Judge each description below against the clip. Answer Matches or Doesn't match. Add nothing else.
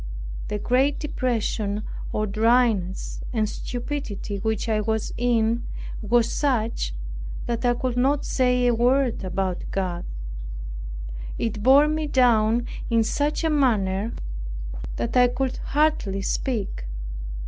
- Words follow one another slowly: Matches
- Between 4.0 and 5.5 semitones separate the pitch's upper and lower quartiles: Doesn't match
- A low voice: Doesn't match